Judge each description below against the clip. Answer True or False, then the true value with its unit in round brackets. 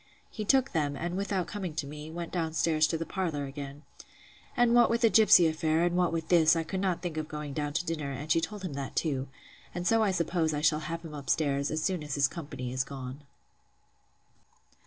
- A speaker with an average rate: False (225 wpm)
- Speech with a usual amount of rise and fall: True (3.3 semitones)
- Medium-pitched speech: True (160 Hz)